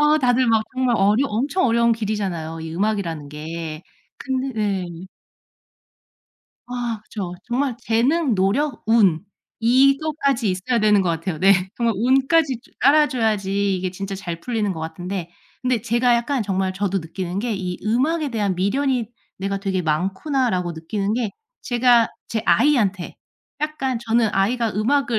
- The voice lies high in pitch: Yes, high, 220 Hz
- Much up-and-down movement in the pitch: No, average, 4.8 semitones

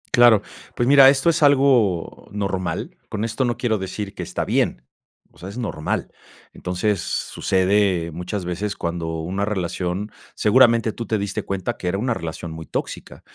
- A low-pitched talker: Yes, low, 100 Hz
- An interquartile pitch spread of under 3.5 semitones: No, average, 4.7 semitones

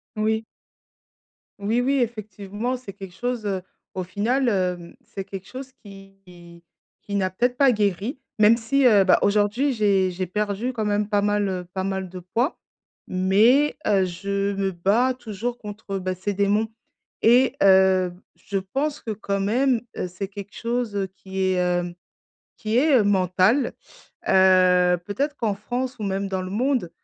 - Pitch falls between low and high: No, high, 205 Hz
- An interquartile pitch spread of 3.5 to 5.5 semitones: Yes, average, 3.8 semitones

